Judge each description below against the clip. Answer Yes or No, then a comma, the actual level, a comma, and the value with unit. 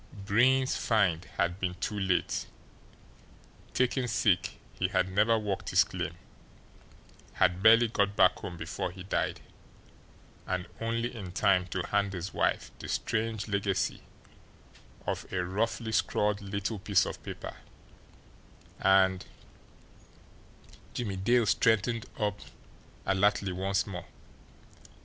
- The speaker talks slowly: Yes, slow, 115 wpm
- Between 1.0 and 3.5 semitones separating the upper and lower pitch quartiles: Yes, average, 3.0 semitones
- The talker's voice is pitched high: No, low, 100 Hz